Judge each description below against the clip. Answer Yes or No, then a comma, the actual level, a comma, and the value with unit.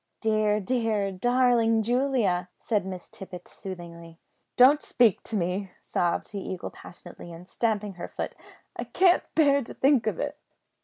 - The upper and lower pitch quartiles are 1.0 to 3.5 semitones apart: No, average, 5.1 semitones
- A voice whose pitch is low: No, high, 210 Hz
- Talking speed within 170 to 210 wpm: No, average, 150 wpm